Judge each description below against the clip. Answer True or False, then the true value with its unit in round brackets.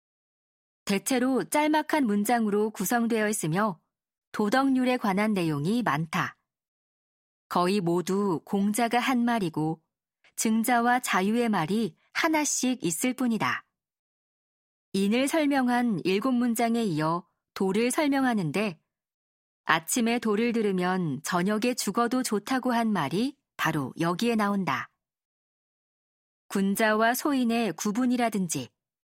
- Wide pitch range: False (4.2 semitones)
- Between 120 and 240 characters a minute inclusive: True (235 characters per minute)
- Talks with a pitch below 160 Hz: False (220 Hz)